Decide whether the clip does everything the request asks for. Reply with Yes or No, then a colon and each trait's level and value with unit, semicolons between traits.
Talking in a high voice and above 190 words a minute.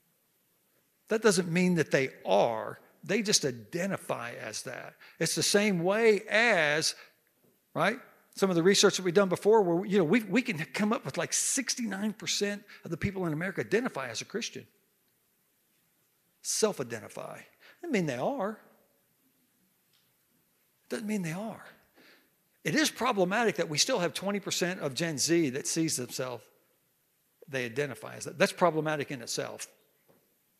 No: high, 195 Hz; average, 155 wpm